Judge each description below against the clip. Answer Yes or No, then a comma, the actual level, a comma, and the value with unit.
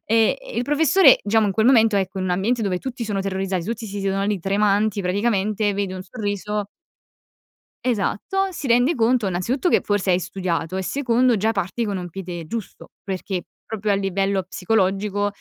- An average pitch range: Yes, average, 3.0 semitones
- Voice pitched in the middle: No, high, 205 Hz